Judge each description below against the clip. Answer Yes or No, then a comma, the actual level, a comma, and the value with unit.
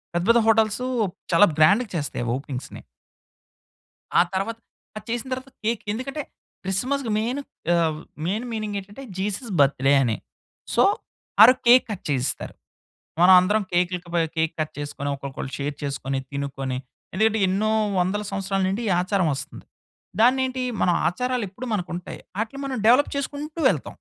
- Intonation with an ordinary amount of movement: No, wide, 6.9 semitones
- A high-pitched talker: Yes, high, 200 Hz